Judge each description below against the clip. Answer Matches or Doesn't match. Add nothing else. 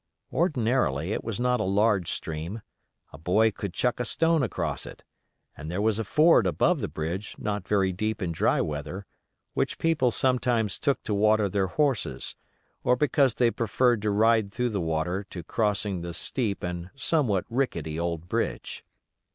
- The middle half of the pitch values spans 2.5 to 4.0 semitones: Doesn't match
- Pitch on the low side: Matches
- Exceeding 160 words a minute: Matches